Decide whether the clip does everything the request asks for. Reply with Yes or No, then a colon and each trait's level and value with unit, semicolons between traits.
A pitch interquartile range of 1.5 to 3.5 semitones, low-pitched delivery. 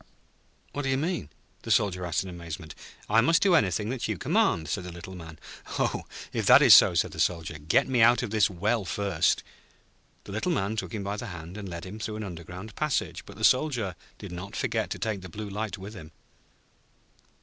No: average, 4.0 semitones; low, 100 Hz